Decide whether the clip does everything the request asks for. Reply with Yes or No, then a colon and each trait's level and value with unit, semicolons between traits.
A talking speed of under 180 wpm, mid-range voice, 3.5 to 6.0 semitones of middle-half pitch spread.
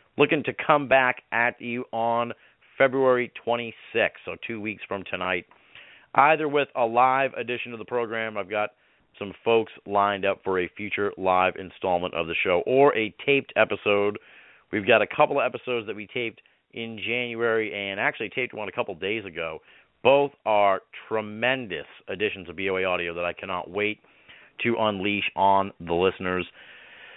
No: average, 170 wpm; low, 110 Hz; average, 3.9 semitones